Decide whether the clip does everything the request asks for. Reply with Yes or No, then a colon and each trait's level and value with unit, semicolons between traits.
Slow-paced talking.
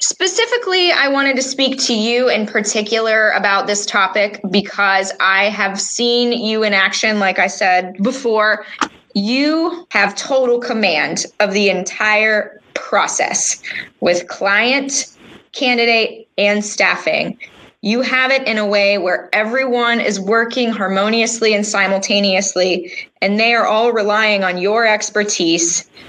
Yes: slow, 130 wpm